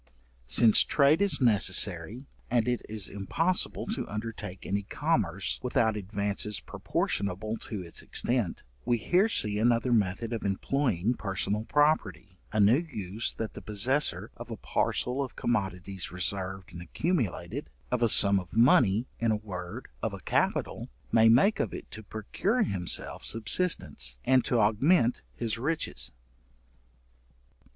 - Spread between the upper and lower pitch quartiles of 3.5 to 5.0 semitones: Yes, average, 4.1 semitones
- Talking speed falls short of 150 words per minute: Yes, average, 140 wpm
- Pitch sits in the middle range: No, low, 110 Hz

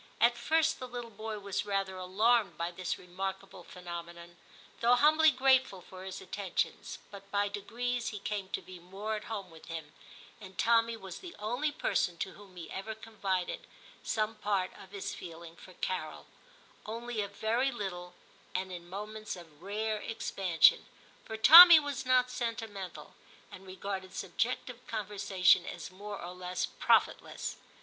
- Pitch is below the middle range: No, high, 200 Hz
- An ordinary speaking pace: Yes, average, 155 wpm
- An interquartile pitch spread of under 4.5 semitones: Yes, average, 3.8 semitones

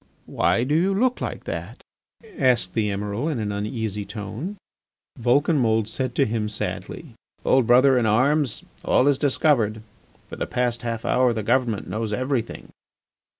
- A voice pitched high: No, low, 120 Hz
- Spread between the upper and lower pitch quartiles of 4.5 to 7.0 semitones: No, average, 4.1 semitones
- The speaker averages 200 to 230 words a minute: No, average, 150 wpm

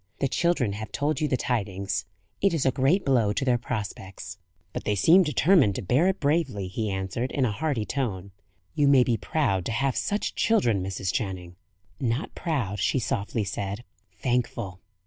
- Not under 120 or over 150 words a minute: No, average, 180 wpm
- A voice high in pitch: No, low, 120 Hz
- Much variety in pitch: Yes, wide, 6.2 semitones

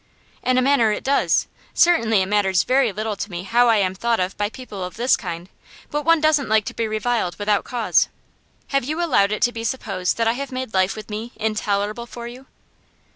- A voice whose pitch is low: No, high, 225 Hz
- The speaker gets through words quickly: Yes, fast, 220 wpm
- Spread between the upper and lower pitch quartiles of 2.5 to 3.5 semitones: No, average, 3.9 semitones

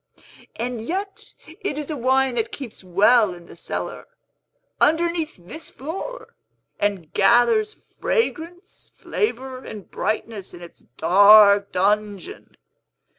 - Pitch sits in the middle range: No, high, 245 Hz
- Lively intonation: Yes, wide, 8.2 semitones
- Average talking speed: No, slow, 115 wpm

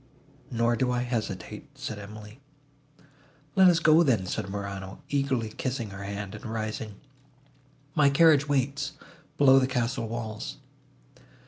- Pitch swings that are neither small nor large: Yes, average, 4.6 semitones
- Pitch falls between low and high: No, low, 115 Hz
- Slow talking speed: Yes, slow, 130 wpm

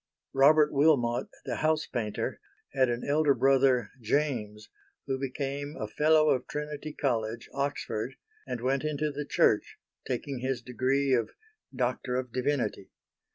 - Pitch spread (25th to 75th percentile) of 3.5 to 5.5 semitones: No, average, 3.0 semitones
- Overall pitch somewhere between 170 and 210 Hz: No, low, 135 Hz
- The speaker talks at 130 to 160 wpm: Yes, slow, 135 wpm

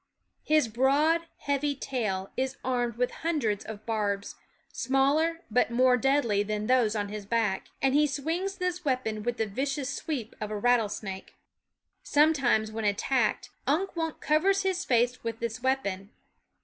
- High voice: Yes, very high, 250 Hz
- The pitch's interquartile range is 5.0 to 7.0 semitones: Yes, average, 5.3 semitones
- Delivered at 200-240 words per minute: No, average, 155 wpm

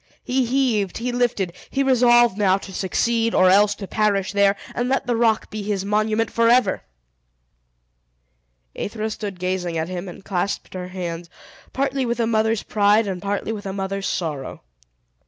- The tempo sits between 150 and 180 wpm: Yes, average, 165 wpm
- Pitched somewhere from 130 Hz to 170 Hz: No, high, 205 Hz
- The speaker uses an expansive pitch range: No, average, 3.4 semitones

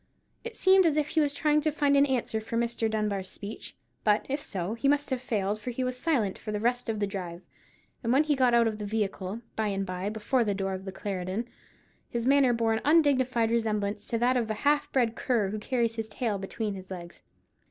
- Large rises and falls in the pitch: No, average, 4.0 semitones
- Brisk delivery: Yes, fast, 235 wpm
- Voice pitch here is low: No, high, 225 Hz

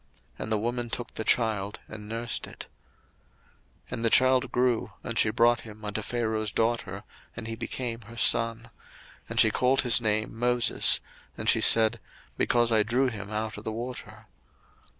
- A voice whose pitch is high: No, low, 115 Hz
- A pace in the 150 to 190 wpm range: Yes, average, 170 wpm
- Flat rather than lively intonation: Yes, narrow, 1.7 semitones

